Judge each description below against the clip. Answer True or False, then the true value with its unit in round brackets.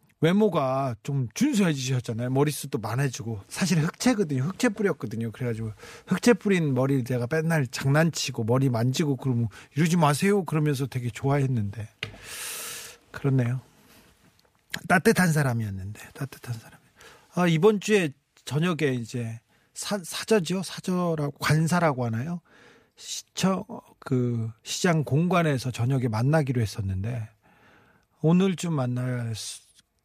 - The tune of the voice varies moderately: False (6.4 semitones)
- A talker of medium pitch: True (145 Hz)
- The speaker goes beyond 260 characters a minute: True (300 characters per minute)